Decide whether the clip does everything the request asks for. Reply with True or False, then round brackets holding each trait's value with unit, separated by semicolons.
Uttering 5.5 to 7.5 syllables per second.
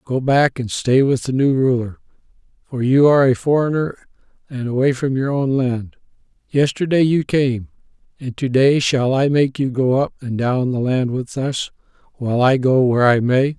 False (4.8 syllables/s)